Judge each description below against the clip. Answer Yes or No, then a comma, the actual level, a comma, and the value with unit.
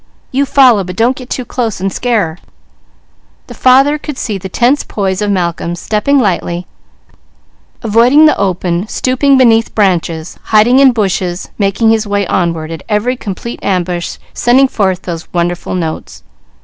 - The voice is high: Yes, high, 210 Hz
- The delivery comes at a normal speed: Yes, average, 155 wpm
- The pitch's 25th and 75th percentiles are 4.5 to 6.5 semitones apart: Yes, wide, 5.6 semitones